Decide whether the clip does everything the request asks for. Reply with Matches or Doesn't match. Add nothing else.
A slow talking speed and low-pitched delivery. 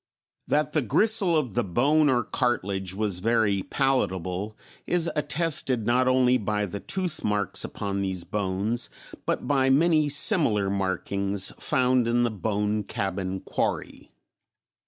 Matches